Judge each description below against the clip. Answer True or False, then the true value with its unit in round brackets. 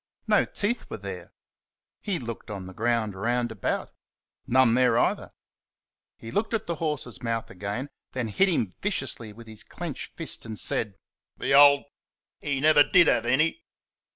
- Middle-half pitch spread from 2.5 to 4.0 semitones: False (5.1 semitones)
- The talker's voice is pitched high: False (120 Hz)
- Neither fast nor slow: True (160 wpm)